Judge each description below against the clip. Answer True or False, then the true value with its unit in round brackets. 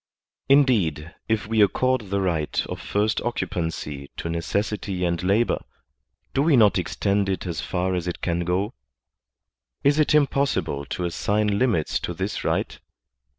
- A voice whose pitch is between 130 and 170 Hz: False (95 Hz)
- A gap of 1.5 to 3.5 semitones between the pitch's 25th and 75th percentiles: False (4.6 semitones)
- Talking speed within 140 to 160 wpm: True (150 wpm)